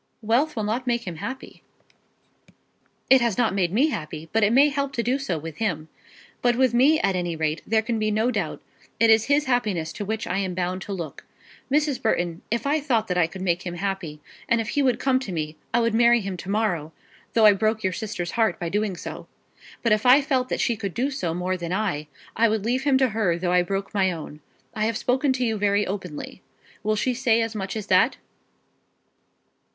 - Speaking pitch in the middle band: No, high, 215 Hz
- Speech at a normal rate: No, fast, 230 wpm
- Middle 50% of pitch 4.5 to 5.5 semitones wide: Yes, average, 5.0 semitones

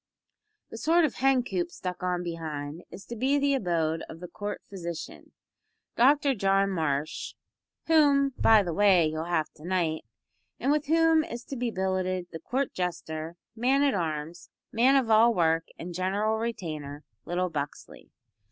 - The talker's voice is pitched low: No, medium, 185 Hz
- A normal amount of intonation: No, wide, 6.9 semitones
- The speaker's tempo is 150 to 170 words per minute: Yes, average, 160 wpm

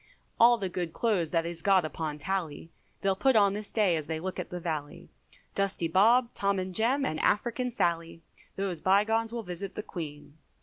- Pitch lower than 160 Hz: No, high, 190 Hz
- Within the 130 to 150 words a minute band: No, average, 200 wpm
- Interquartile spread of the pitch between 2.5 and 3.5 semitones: No, average, 4.3 semitones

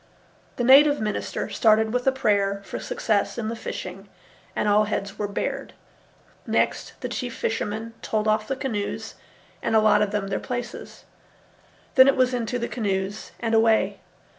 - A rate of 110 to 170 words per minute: Yes, average, 160 wpm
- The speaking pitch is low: No, high, 220 Hz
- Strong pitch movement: No, average, 3.0 semitones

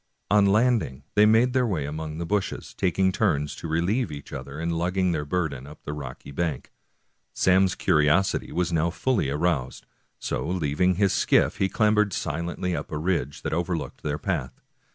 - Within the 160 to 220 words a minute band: Yes, average, 175 wpm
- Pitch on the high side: No, very low, 85 Hz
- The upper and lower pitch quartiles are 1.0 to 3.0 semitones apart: No, average, 4.5 semitones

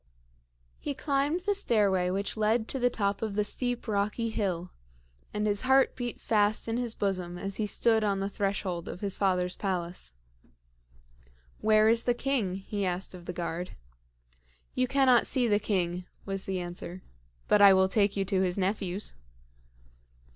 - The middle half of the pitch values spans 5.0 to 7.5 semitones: No, average, 3.4 semitones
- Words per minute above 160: Yes, average, 170 wpm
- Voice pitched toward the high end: Yes, high, 205 Hz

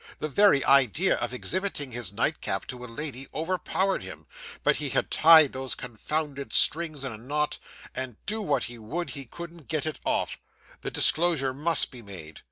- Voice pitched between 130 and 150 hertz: Yes, medium, 140 Hz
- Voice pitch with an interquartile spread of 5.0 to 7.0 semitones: No, average, 4.6 semitones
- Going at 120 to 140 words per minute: No, average, 175 wpm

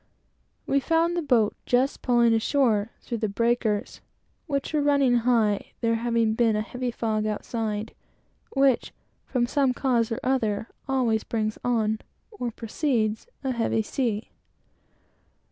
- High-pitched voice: Yes, high, 235 Hz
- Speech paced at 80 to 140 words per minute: Yes, slow, 135 wpm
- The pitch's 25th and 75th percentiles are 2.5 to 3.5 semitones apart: Yes, average, 3.1 semitones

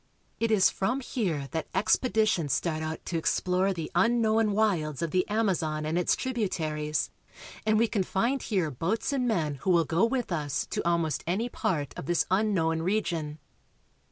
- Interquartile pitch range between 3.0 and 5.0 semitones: No, wide, 5.4 semitones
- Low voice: No, medium, 180 Hz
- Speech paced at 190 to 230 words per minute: No, average, 170 wpm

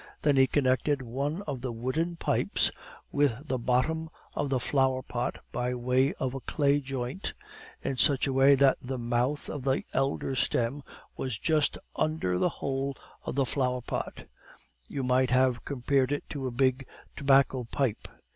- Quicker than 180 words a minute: No, average, 165 wpm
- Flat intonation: Yes, narrow, 1.9 semitones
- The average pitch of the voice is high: No, low, 135 Hz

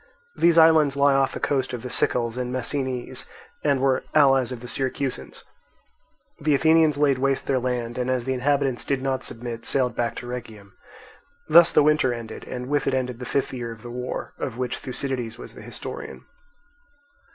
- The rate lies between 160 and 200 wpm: Yes, average, 185 wpm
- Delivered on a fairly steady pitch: Yes, narrow, 2.2 semitones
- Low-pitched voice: Yes, low, 130 Hz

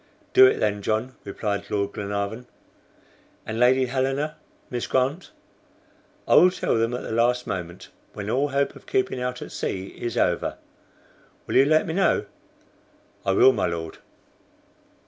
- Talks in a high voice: No, low, 125 Hz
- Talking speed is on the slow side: No, average, 155 wpm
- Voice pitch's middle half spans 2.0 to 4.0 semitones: No, average, 4.9 semitones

